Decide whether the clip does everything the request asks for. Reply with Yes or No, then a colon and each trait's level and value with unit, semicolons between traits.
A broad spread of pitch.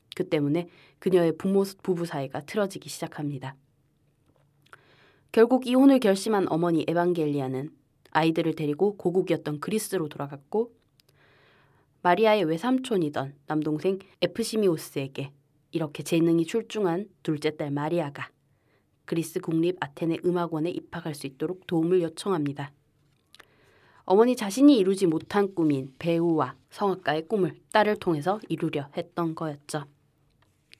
No: average, 4.4 semitones